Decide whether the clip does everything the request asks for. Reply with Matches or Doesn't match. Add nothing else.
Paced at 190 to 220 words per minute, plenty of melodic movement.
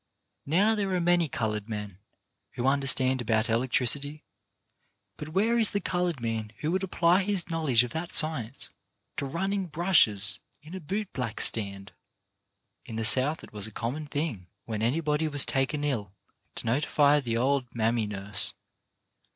Doesn't match